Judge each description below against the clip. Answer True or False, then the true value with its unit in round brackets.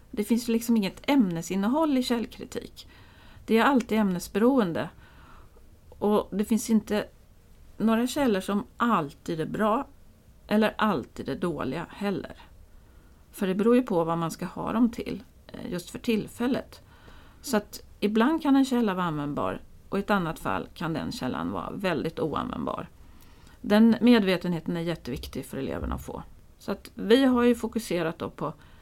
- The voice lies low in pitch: False (210 Hz)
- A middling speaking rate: True (155 wpm)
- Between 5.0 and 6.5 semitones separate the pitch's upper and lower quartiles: True (5.3 semitones)